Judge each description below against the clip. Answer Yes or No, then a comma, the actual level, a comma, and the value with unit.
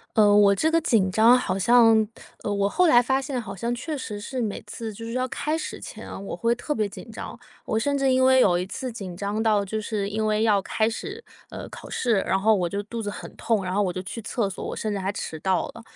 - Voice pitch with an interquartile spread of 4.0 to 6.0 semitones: No, average, 3.4 semitones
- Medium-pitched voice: No, high, 220 Hz